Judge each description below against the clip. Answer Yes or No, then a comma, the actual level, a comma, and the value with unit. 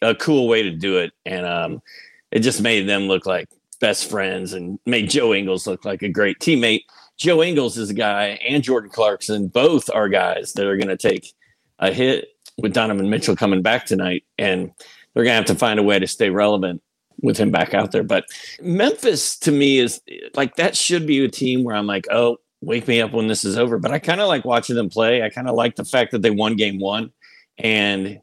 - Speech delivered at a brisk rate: Yes, fast, 230 wpm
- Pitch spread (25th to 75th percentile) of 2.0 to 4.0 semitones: No, average, 5.1 semitones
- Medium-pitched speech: No, low, 115 Hz